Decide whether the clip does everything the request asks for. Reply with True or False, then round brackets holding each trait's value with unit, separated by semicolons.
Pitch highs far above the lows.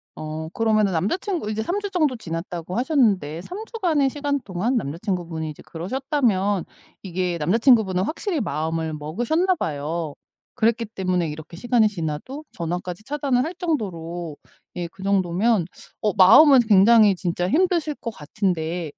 True (7.4 semitones)